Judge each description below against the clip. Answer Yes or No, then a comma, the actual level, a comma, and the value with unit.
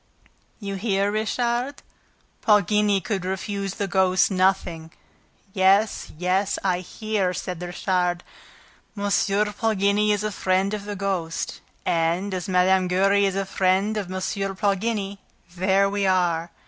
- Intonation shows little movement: Yes, narrow, 1.8 semitones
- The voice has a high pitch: Yes, high, 195 Hz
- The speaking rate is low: Yes, slow, 130 wpm